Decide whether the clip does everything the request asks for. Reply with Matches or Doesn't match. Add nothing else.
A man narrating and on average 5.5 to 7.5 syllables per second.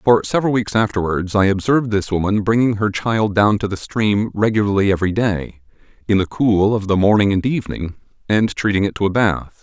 Matches